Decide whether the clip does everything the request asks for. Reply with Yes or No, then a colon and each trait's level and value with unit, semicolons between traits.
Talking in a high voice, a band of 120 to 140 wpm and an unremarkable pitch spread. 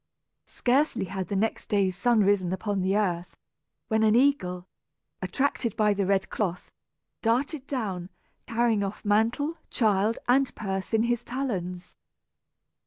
Yes: high, 210 Hz; slow, 135 wpm; average, 4.0 semitones